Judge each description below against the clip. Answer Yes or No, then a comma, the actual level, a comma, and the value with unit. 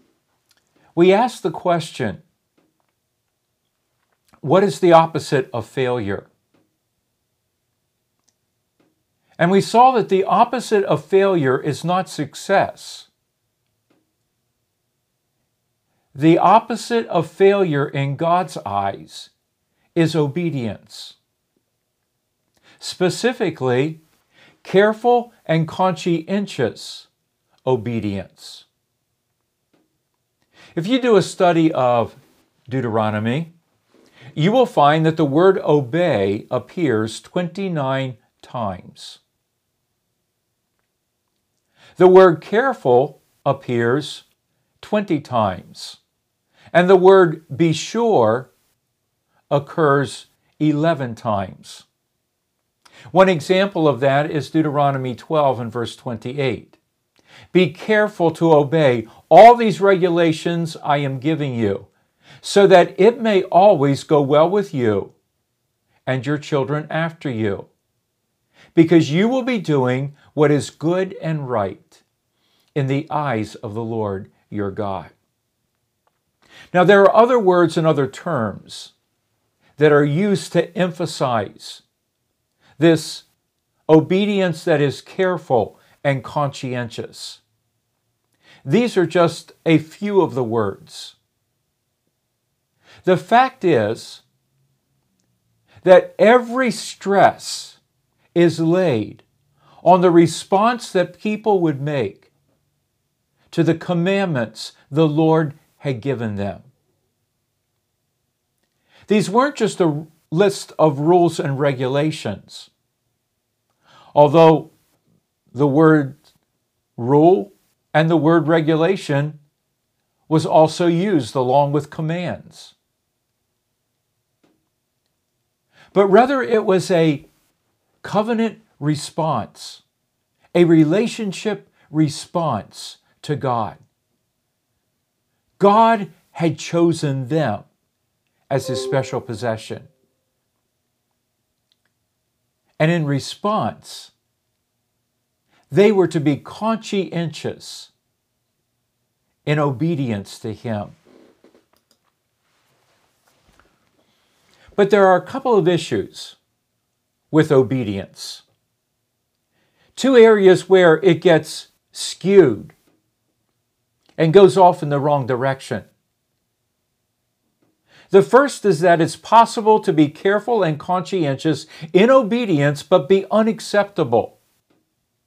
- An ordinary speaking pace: No, slow, 90 wpm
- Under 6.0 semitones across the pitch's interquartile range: No, wide, 6.7 semitones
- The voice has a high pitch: No, medium, 150 Hz